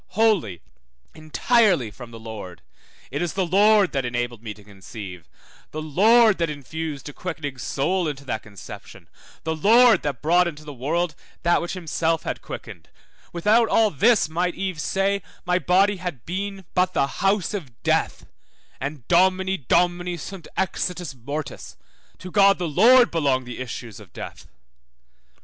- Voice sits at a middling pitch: Yes, medium, 170 Hz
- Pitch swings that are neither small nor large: No, wide, 5.7 semitones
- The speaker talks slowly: No, average, 155 wpm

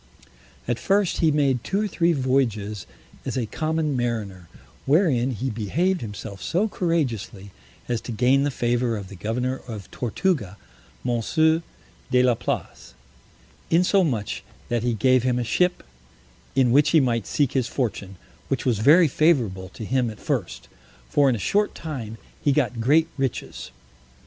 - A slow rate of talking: No, average, 155 wpm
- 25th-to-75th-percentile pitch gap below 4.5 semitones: No, average, 5.3 semitones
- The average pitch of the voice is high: No, low, 125 Hz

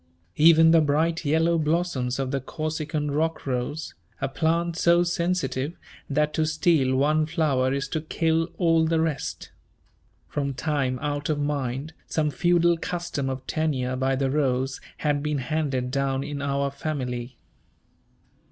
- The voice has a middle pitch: Yes, medium, 150 Hz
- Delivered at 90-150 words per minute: Yes, average, 145 wpm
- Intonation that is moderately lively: Yes, average, 3.3 semitones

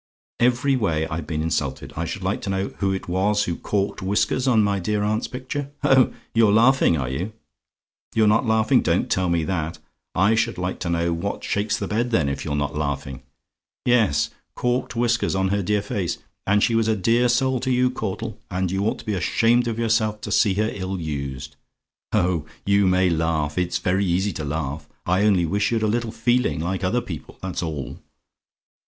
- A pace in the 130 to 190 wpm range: No, average, 200 wpm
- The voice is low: Yes, low, 100 Hz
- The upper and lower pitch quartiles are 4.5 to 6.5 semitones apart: Yes, average, 5.0 semitones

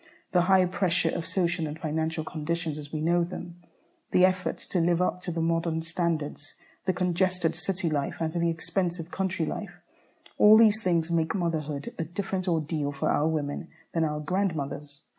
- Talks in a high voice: No, medium, 170 Hz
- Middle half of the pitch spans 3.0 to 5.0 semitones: No, narrow, 2.4 semitones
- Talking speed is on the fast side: No, average, 175 wpm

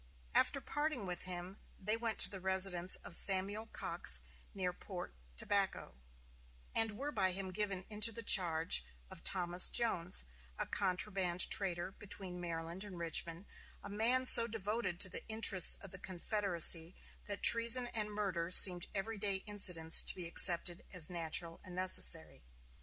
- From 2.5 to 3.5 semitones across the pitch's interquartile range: Yes, average, 2.9 semitones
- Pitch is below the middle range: No, high, 190 Hz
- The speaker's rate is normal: Yes, average, 150 wpm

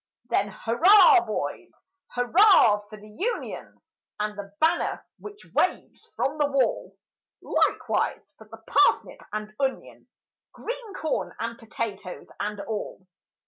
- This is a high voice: Yes, high, 240 Hz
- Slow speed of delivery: Yes, slow, 120 wpm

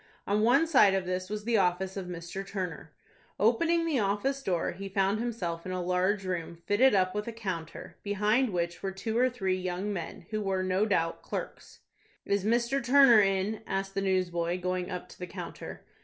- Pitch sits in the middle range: No, high, 195 Hz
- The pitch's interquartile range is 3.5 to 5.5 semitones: No, average, 3.0 semitones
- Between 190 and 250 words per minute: Yes, average, 195 wpm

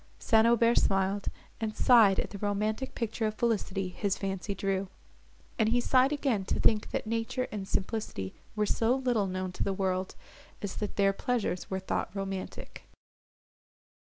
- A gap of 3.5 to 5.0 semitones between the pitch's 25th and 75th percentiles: No, average, 2.9 semitones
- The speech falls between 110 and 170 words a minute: Yes, average, 160 wpm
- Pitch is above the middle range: Yes, high, 205 Hz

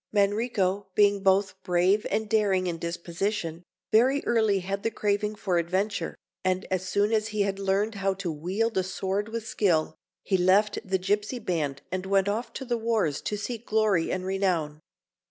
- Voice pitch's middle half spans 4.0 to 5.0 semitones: No, narrow, 2.4 semitones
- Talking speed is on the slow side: No, average, 175 wpm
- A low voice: No, high, 195 Hz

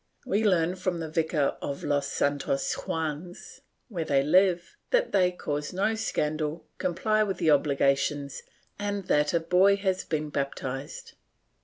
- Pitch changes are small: No, average, 4.4 semitones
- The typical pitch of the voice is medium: Yes, medium, 165 Hz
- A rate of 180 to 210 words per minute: No, average, 145 wpm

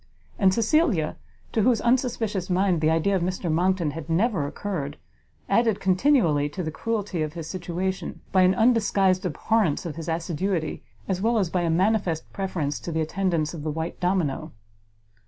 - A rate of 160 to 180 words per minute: Yes, average, 170 wpm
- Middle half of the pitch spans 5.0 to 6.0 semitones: No, average, 3.7 semitones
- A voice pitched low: No, medium, 185 Hz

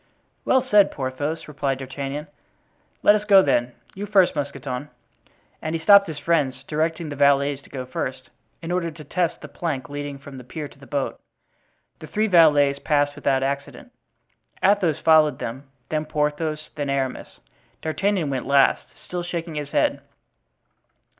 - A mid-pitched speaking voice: Yes, medium, 150 Hz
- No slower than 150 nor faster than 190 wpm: Yes, average, 160 wpm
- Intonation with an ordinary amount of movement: Yes, average, 3.2 semitones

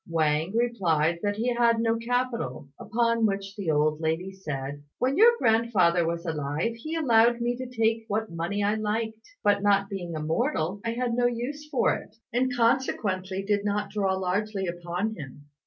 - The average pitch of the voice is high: Yes, high, 205 Hz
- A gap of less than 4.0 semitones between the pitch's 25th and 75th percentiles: No, average, 5.3 semitones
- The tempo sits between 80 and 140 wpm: No, average, 175 wpm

